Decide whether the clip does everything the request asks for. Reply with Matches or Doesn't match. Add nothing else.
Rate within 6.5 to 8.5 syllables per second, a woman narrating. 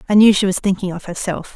Matches